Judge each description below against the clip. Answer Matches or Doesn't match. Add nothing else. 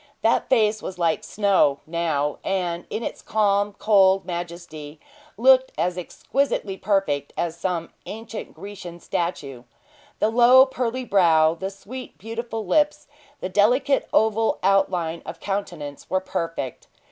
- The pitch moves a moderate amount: Matches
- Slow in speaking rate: Matches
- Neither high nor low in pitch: Doesn't match